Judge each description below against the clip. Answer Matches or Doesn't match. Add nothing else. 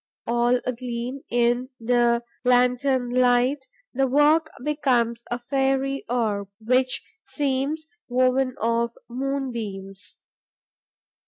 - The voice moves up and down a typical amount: Doesn't match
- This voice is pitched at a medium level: Doesn't match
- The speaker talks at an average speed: Doesn't match